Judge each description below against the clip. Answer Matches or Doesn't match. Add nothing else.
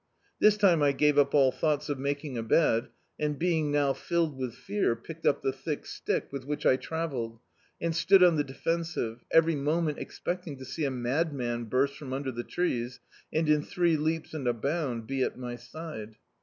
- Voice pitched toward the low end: Doesn't match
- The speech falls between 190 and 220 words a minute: Matches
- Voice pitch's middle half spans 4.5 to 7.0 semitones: Doesn't match